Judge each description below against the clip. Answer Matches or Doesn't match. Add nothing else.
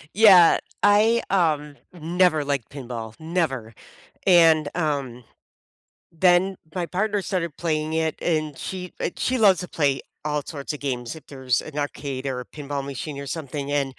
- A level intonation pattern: Doesn't match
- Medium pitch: Matches